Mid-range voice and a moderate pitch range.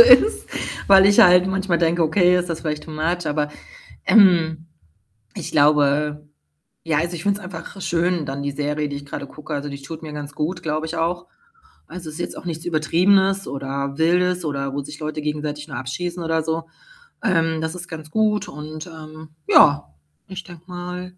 Yes: medium, 160 Hz; average, 3.1 semitones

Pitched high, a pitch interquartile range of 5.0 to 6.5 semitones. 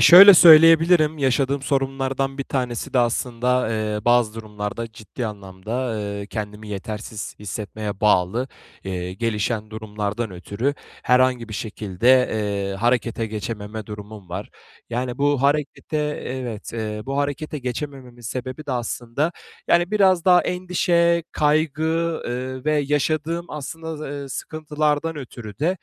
No: low, 125 Hz; wide, 5.5 semitones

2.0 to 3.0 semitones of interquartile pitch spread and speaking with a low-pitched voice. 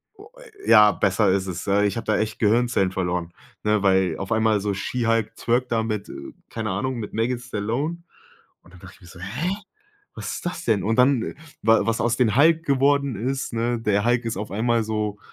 No: average, 3.5 semitones; low, 110 Hz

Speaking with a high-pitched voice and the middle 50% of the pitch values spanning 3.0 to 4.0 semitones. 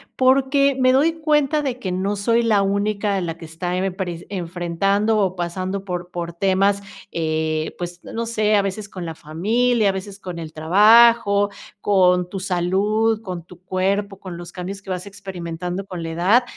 Yes: high, 195 Hz; average, 3.3 semitones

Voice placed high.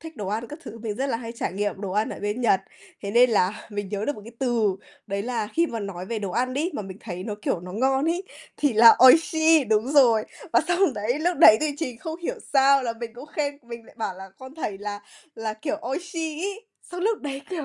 Yes: high, 235 Hz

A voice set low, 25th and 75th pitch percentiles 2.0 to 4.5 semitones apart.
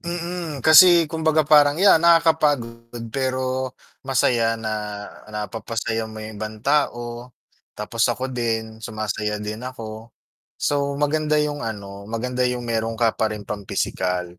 No: low, 120 Hz; average, 5.0 semitones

